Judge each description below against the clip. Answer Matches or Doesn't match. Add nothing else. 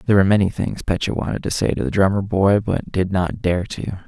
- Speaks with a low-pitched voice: Matches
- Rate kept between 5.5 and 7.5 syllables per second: Matches